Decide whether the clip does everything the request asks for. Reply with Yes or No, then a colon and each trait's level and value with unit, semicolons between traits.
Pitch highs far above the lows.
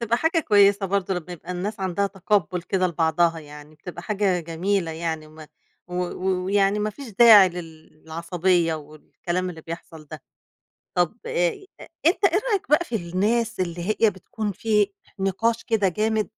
No: average, 3.9 semitones